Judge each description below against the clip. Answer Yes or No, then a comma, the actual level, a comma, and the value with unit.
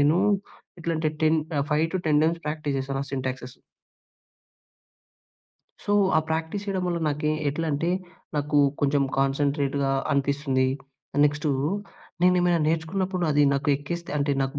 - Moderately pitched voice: Yes, medium, 150 Hz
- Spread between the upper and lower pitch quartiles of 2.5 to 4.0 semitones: Yes, average, 2.8 semitones